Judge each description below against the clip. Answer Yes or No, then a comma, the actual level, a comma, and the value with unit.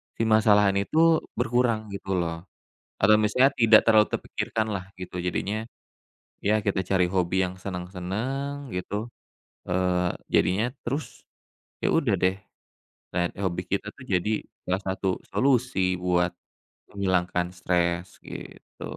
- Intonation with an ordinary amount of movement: Yes, average, 3.4 semitones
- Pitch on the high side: No, low, 100 Hz